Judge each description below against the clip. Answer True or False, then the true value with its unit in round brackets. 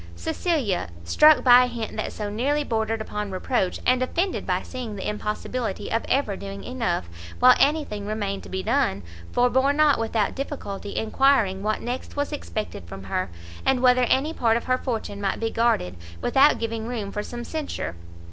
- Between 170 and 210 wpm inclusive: True (175 wpm)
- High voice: True (230 Hz)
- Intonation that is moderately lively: True (4.3 semitones)